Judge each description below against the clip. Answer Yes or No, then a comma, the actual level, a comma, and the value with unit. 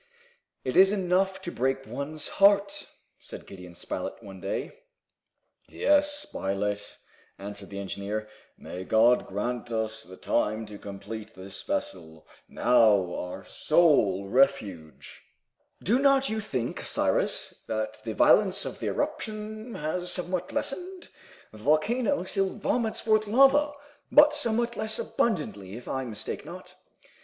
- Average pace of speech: No, slow, 130 wpm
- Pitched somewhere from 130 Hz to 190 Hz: Yes, low, 135 Hz